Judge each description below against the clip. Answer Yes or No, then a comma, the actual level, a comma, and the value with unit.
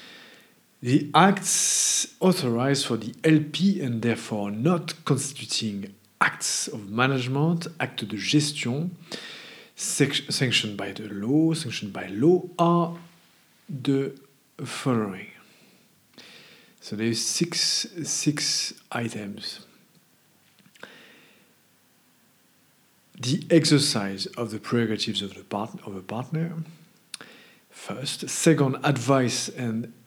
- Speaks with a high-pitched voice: No, medium, 140 Hz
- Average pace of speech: No, slow, 90 wpm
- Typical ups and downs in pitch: No, wide, 6.4 semitones